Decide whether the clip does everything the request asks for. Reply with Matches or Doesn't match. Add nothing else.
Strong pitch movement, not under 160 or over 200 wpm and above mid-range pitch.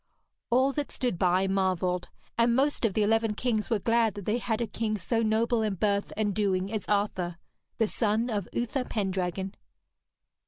Doesn't match